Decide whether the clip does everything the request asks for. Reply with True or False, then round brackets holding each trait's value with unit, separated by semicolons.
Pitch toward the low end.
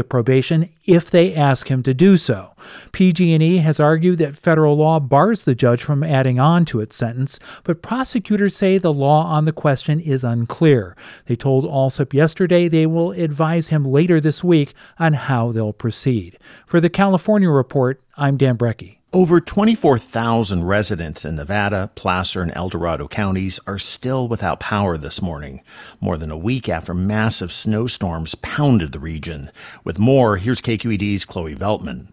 True (130 Hz)